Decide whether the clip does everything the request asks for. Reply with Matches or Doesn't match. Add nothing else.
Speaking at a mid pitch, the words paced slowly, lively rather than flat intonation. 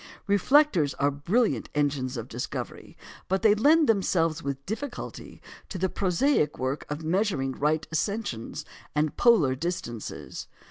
Matches